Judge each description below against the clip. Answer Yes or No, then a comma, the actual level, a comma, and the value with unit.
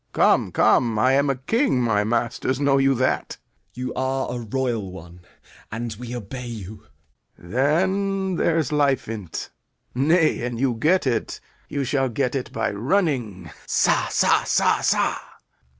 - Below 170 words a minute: Yes, average, 155 wpm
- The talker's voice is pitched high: No, low, 125 Hz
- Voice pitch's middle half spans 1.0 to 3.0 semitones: No, average, 3.8 semitones